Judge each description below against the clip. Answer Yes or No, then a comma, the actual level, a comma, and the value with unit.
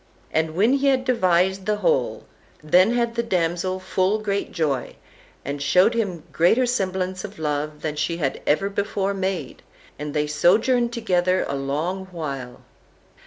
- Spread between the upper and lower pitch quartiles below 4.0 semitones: No, average, 5.3 semitones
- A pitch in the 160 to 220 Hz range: Yes, medium, 185 Hz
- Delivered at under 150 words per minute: No, average, 155 wpm